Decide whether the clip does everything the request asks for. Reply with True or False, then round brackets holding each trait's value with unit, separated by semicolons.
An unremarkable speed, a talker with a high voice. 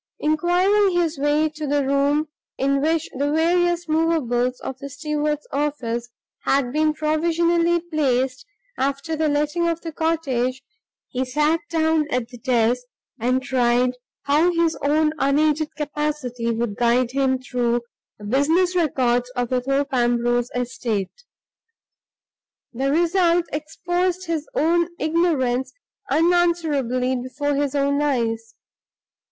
False (125 wpm; 290 Hz)